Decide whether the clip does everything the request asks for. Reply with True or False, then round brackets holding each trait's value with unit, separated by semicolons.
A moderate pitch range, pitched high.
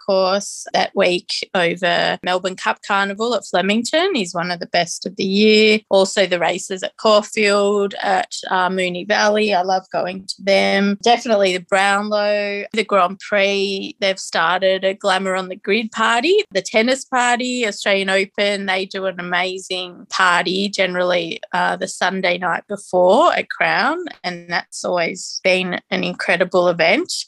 False (2.2 semitones; 195 Hz)